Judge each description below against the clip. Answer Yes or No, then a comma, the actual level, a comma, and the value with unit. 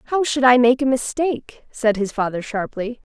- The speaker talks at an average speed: Yes, average, 190 wpm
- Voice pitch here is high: Yes, high, 245 Hz